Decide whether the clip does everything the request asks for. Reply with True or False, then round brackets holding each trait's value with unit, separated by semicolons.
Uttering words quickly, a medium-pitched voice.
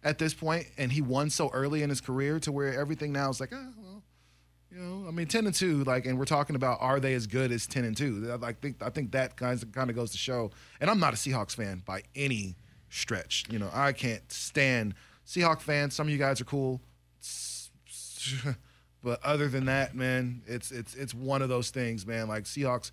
False (230 wpm; 130 Hz)